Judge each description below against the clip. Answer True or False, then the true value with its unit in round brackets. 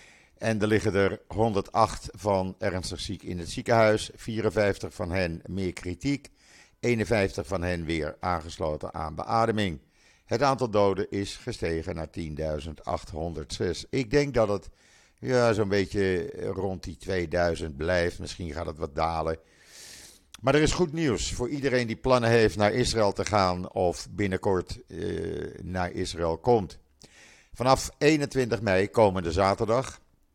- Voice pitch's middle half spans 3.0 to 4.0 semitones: False (4.8 semitones)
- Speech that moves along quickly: False (140 wpm)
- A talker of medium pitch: False (95 Hz)